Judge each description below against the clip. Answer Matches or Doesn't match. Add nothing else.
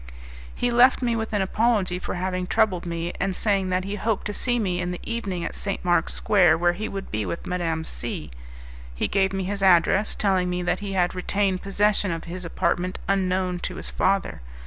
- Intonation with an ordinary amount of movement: Doesn't match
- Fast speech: Matches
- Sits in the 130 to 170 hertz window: Doesn't match